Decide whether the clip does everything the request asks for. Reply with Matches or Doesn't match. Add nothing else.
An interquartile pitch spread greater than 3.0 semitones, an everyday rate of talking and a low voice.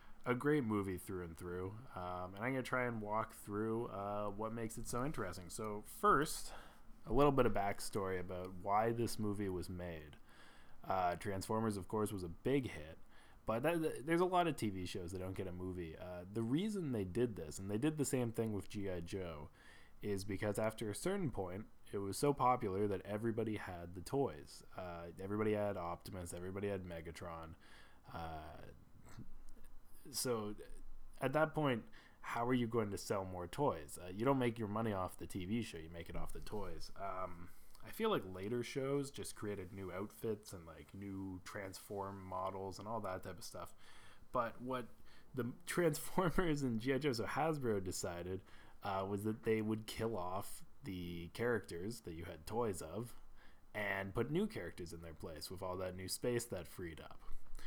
Matches